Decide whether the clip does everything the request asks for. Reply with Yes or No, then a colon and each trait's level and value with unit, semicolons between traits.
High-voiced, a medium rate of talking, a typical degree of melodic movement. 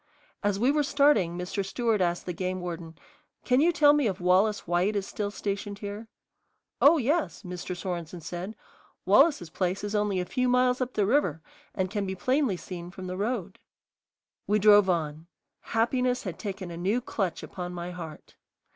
Yes: high, 195 Hz; average, 180 wpm; average, 4.6 semitones